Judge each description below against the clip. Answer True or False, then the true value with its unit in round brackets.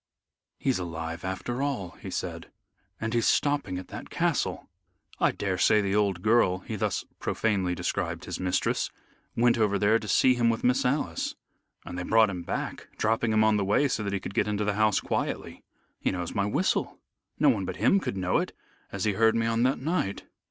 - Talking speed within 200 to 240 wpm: True (205 wpm)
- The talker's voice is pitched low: True (105 Hz)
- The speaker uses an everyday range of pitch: True (3.5 semitones)